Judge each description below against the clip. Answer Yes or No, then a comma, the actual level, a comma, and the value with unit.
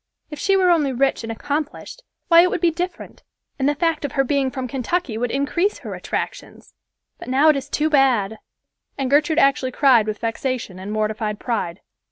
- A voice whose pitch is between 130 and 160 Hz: No, very high, 275 Hz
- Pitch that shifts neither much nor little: Yes, average, 4.9 semitones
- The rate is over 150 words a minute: Yes, average, 195 wpm